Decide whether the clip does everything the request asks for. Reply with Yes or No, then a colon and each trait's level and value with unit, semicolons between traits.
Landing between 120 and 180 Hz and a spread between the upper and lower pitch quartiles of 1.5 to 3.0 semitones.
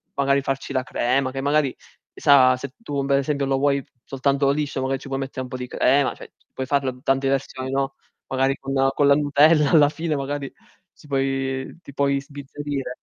No: low, 135 Hz; narrow, 1.0 semitones